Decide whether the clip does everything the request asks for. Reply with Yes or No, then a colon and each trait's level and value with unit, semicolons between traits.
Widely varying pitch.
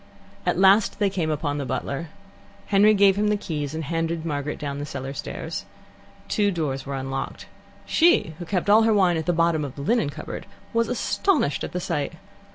Yes: wide, 5.7 semitones